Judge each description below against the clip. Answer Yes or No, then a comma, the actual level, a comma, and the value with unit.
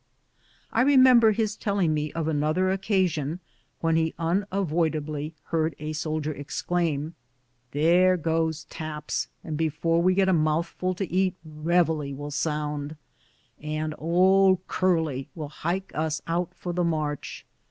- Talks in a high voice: No, medium, 160 Hz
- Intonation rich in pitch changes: No, average, 3.2 semitones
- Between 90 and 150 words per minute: Yes, average, 140 wpm